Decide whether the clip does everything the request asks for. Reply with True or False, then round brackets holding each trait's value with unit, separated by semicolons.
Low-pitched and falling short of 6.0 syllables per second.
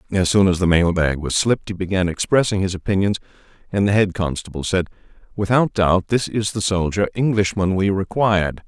True (95 Hz; 5.6 syllables/s)